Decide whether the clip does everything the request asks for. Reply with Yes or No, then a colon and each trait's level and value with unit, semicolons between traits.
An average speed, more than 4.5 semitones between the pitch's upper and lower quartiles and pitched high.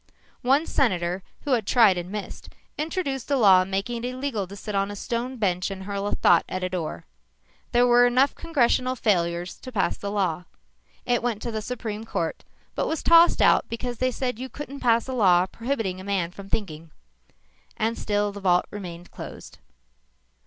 Yes: average, 190 wpm; average, 4.9 semitones; high, 215 Hz